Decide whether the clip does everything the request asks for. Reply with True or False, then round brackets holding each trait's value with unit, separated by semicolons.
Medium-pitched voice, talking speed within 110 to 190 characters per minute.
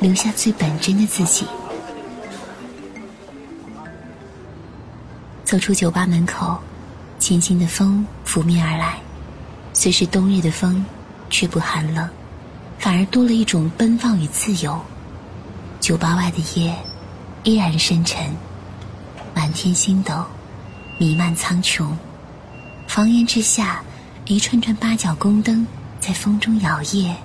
True (175 Hz; 165 characters per minute)